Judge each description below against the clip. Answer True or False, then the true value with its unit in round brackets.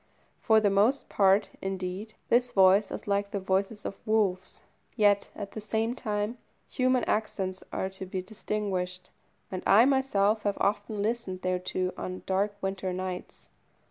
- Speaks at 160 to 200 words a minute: False (150 wpm)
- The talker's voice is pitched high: True (200 Hz)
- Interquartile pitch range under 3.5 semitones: True (2.4 semitones)